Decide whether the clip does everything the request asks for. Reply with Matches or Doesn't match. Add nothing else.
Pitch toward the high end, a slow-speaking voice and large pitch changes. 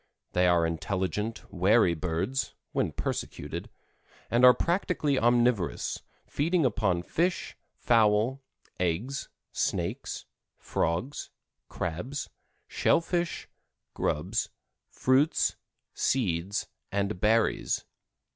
Doesn't match